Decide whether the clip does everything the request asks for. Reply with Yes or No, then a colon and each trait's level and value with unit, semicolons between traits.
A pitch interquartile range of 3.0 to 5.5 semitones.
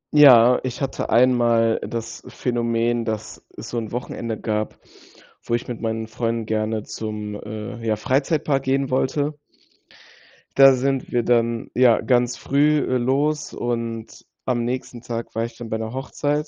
No: narrow, 2.4 semitones